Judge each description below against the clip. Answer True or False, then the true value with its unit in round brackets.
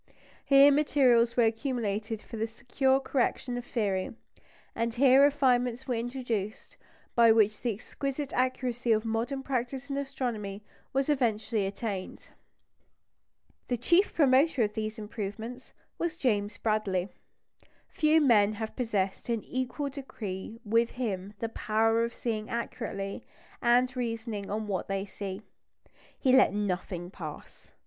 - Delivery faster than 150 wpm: False (135 wpm)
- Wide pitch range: False (3.5 semitones)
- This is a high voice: True (230 Hz)